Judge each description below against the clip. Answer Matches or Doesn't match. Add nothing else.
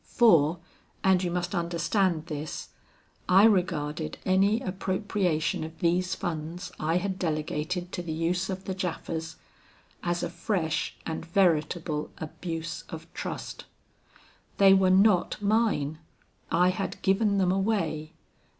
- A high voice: Doesn't match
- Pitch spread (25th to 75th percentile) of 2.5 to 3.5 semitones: Matches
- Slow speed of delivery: Matches